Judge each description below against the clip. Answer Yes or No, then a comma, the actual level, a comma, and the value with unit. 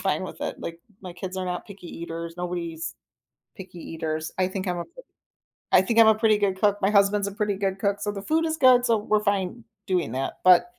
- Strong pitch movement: No, average, 2.8 semitones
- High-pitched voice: Yes, high, 195 Hz